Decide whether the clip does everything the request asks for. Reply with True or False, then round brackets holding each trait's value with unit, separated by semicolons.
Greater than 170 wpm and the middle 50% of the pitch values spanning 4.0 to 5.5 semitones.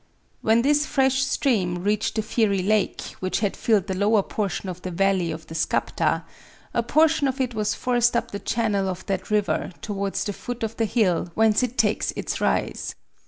False (195 wpm; 3.4 semitones)